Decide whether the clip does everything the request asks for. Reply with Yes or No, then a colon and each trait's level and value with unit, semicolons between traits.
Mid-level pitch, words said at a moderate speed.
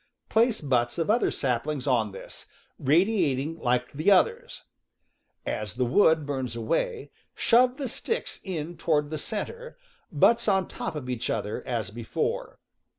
Yes: medium, 150 Hz; average, 145 wpm